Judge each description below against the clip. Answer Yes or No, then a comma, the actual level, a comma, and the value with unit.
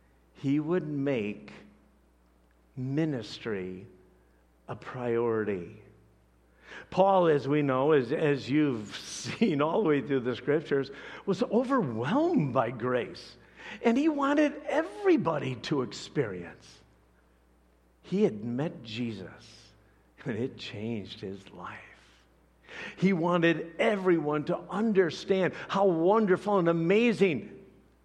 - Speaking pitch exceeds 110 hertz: Yes, low, 135 Hz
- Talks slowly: Yes, slow, 105 wpm